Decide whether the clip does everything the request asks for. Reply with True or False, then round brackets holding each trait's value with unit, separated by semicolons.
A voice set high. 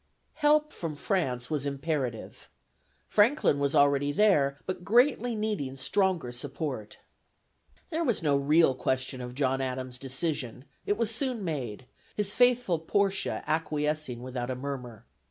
False (145 Hz)